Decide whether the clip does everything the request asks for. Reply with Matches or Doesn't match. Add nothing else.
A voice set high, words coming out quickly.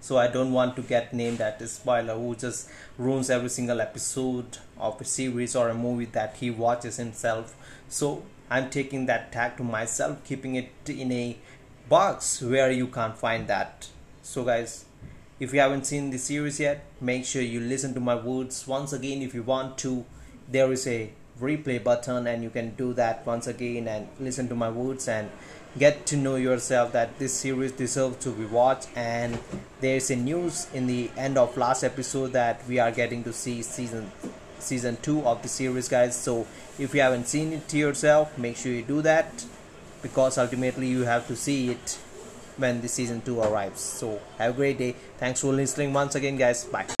Doesn't match